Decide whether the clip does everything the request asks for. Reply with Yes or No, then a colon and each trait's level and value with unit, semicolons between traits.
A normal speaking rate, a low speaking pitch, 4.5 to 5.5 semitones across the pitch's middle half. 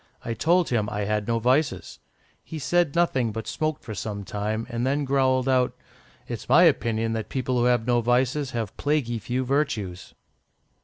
No: average, 175 wpm; low, 125 Hz; average, 3.7 semitones